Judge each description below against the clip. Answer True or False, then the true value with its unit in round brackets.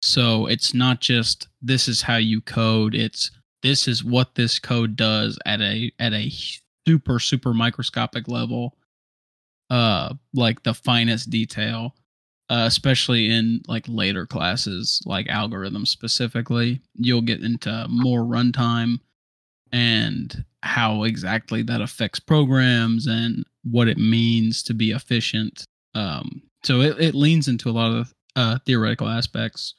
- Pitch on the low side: True (115 Hz)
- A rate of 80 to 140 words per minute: True (135 wpm)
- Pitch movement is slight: True (1.7 semitones)